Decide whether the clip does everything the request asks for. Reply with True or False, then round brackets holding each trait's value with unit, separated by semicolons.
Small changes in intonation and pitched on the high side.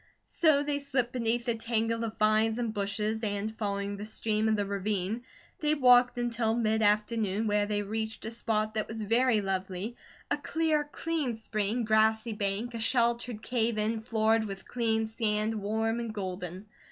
True (2.0 semitones; 220 Hz)